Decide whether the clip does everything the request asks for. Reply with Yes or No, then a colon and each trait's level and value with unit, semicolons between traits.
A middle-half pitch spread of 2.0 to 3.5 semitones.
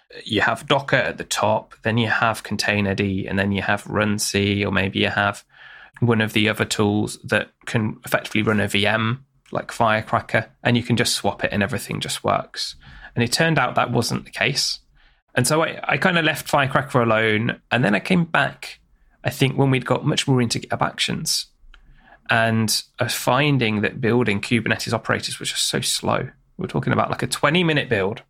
No: average, 4.1 semitones